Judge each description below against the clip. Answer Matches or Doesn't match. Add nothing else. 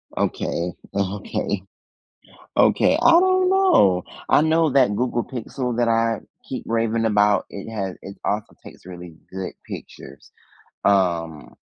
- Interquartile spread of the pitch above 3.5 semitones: Matches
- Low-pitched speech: Matches